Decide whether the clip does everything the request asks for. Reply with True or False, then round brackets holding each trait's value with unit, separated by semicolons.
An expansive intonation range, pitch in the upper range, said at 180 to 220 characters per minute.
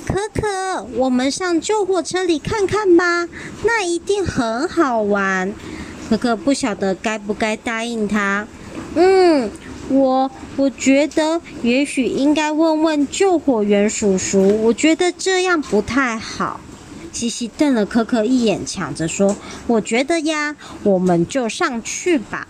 True (7.2 semitones; 270 Hz; 195 characters per minute)